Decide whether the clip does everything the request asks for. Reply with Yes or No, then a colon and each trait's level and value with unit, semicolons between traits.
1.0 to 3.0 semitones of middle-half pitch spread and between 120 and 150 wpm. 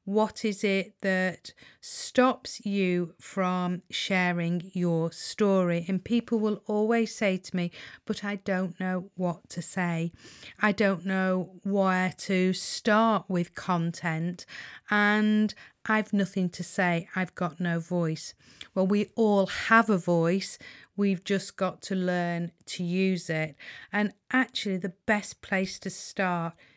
Yes: average, 2.7 semitones; average, 140 wpm